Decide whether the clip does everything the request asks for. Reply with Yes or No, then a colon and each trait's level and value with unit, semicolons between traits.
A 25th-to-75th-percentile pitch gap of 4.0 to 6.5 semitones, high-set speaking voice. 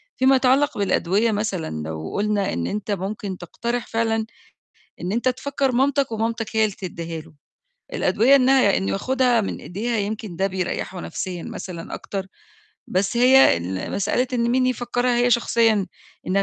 Yes: average, 4.3 semitones; high, 220 Hz